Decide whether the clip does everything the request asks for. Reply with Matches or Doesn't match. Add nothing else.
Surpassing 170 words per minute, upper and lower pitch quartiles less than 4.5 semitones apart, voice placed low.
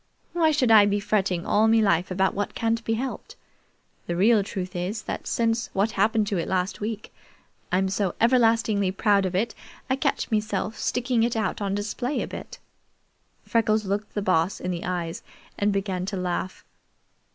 Doesn't match